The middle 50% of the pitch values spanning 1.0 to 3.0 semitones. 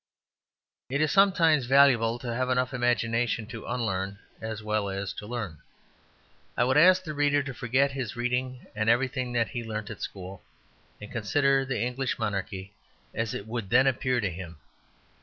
No: average, 3.6 semitones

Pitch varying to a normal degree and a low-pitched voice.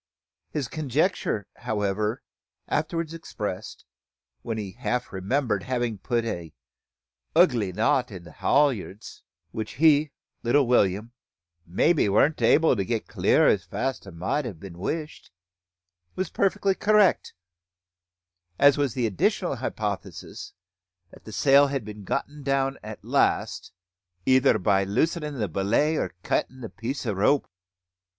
No: wide, 5.9 semitones; low, 120 Hz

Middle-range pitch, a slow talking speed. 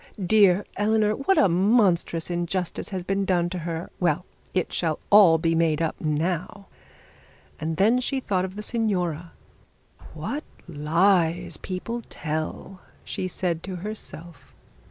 Yes: medium, 180 Hz; slow, 130 wpm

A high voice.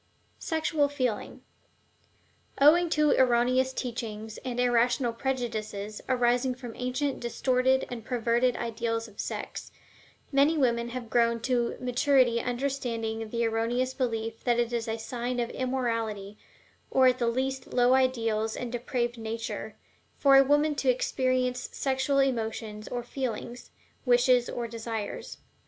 Yes: high, 245 Hz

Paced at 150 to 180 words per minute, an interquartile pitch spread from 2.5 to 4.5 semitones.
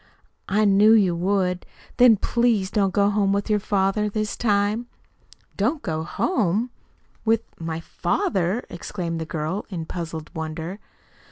No: average, 140 wpm; average, 3.8 semitones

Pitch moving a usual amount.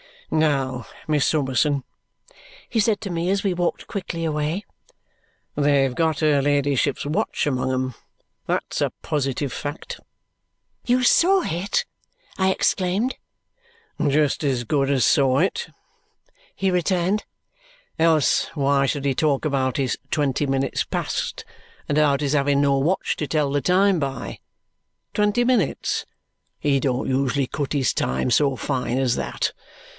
Yes: average, 4.2 semitones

